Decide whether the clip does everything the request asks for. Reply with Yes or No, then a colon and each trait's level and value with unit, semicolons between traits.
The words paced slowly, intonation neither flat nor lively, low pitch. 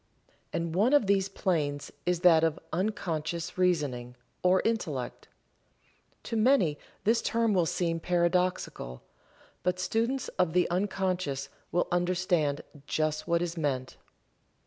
No: slow, 125 wpm; average, 3.3 semitones; medium, 175 Hz